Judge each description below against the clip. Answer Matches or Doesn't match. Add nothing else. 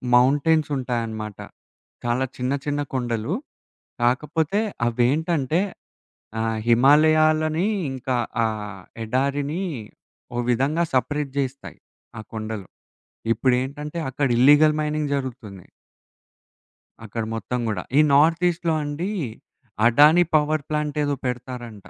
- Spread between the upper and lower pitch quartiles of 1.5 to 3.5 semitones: Doesn't match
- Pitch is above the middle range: Doesn't match